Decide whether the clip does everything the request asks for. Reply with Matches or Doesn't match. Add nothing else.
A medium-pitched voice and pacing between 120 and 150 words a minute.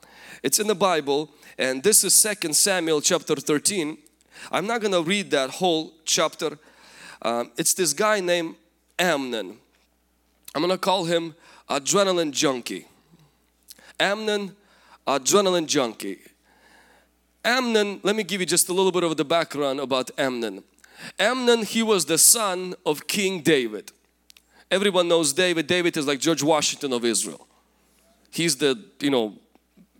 Matches